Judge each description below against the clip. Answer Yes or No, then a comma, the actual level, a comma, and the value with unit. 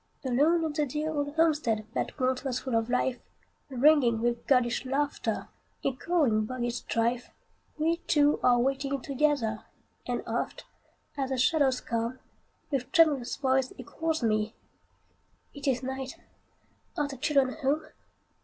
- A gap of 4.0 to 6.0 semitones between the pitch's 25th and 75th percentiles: No, average, 3.3 semitones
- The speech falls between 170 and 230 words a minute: No, average, 140 wpm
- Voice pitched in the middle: No, very high, 265 Hz